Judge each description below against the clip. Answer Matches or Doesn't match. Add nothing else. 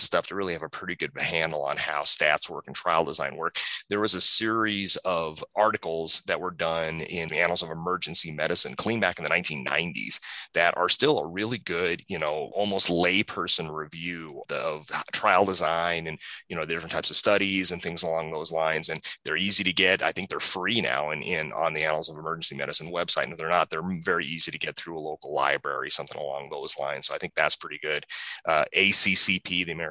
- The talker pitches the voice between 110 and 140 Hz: Doesn't match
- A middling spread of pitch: Matches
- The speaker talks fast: Matches